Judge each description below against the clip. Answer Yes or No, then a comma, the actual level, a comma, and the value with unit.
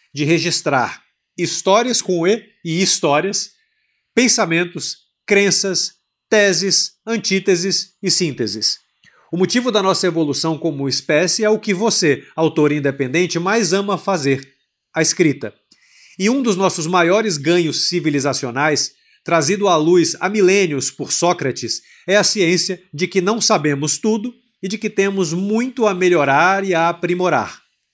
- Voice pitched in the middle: Yes, medium, 180 Hz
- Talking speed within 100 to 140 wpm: Yes, average, 135 wpm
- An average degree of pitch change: Yes, average, 3.7 semitones